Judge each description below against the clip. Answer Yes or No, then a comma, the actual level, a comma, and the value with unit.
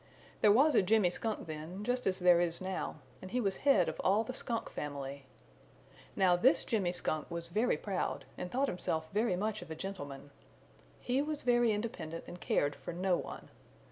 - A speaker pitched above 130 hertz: Yes, high, 190 Hz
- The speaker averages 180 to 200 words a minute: Yes, average, 190 wpm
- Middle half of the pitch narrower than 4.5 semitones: No, average, 4.9 semitones